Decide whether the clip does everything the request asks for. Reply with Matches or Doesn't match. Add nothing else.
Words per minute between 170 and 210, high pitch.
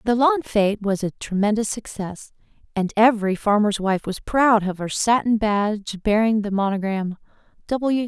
Doesn't match